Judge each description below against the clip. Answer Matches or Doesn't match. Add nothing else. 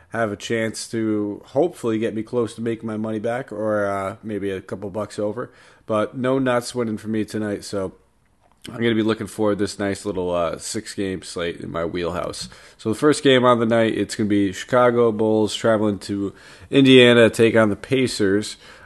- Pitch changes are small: Matches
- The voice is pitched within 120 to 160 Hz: Doesn't match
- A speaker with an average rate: Matches